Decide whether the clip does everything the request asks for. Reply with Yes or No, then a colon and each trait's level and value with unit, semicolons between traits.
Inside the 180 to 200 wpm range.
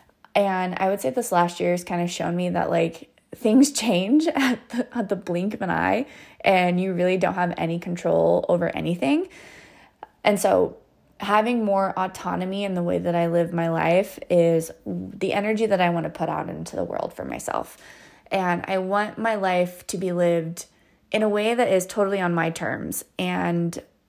Yes: average, 195 wpm